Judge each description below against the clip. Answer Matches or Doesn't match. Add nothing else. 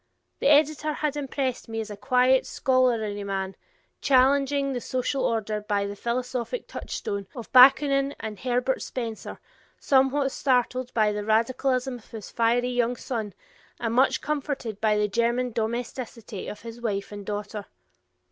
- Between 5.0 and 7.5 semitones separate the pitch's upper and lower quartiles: Doesn't match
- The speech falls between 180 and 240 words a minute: Doesn't match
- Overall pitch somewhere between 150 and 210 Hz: Doesn't match